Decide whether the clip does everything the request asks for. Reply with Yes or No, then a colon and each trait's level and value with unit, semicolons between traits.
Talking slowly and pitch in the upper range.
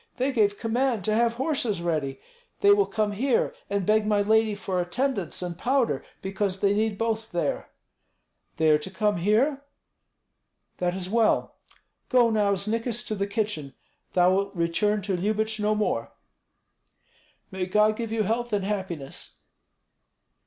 No: average, 150 wpm; high, 210 Hz